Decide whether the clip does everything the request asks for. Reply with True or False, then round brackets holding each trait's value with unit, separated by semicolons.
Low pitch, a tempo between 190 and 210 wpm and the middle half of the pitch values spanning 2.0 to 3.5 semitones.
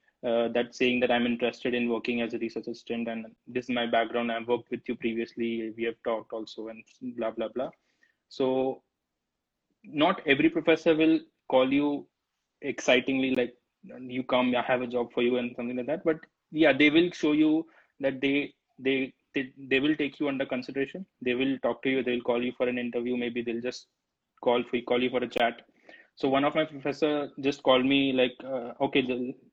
True (125 Hz; 205 wpm; 2.5 semitones)